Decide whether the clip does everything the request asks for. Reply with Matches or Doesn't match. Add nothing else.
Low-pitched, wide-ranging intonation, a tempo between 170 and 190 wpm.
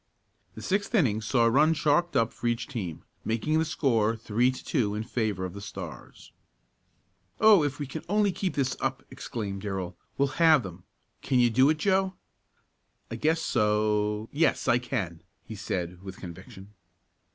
Matches